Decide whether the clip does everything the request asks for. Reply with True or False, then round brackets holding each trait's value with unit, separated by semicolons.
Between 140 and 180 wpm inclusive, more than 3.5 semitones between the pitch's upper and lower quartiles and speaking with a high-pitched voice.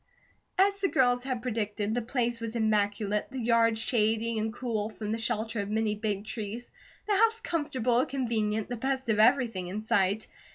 False (175 wpm; 2.6 semitones; 225 Hz)